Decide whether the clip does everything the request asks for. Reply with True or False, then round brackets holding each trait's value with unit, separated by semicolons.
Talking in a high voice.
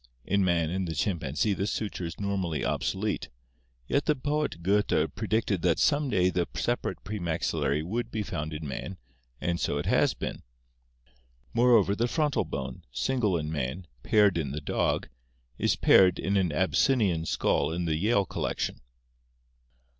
False (95 Hz)